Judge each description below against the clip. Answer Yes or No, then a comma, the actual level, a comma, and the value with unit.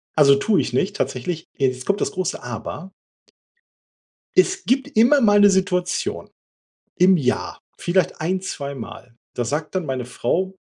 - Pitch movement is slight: No, wide, 6.3 semitones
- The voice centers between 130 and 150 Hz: No, medium, 180 Hz